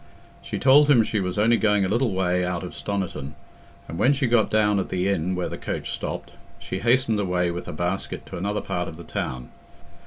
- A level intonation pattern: No, average, 3.9 semitones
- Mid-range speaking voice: No, low, 100 Hz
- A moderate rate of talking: No, fast, 220 wpm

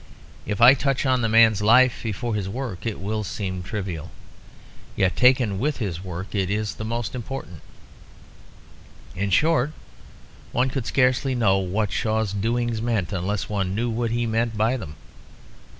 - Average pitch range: Yes, average, 3.7 semitones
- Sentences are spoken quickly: No, average, 155 wpm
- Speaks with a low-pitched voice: Yes, low, 110 Hz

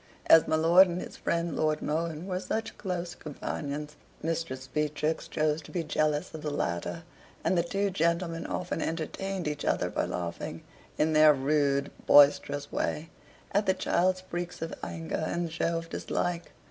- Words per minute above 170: No, average, 165 wpm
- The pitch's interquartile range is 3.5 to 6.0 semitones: No, narrow, 2.6 semitones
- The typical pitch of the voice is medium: Yes, medium, 160 Hz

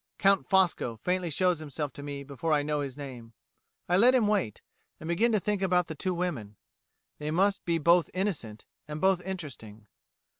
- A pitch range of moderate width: Yes, average, 4.9 semitones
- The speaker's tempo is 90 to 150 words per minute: No, average, 185 wpm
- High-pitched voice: No, medium, 165 Hz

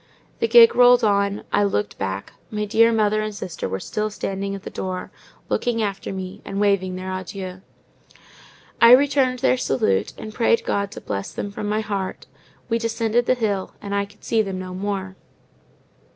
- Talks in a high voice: Yes, high, 205 Hz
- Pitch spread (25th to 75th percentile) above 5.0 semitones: No, average, 3.1 semitones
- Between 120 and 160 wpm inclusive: No, average, 180 wpm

